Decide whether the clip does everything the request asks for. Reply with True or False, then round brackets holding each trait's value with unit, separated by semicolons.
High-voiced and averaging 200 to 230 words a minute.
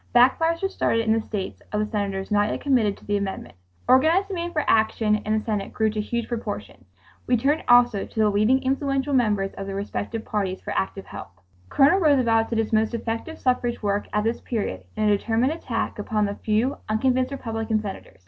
True (225 Hz; 205 wpm)